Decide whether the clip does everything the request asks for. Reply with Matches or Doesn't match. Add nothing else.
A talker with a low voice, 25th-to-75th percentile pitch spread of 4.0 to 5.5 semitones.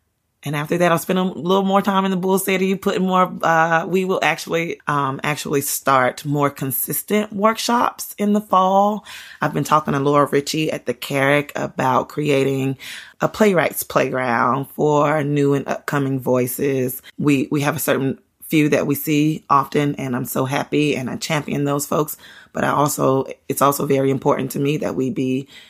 Doesn't match